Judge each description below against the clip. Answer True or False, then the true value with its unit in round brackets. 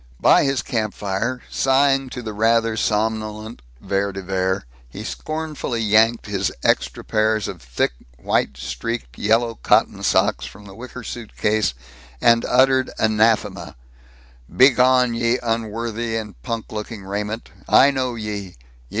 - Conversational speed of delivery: False (130 wpm)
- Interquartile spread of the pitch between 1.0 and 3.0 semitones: True (2.5 semitones)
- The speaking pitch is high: False (110 Hz)